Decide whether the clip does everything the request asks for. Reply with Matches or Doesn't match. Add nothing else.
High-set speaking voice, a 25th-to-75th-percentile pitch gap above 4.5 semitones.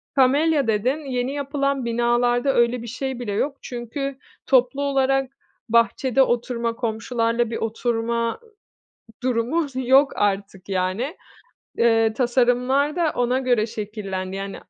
Doesn't match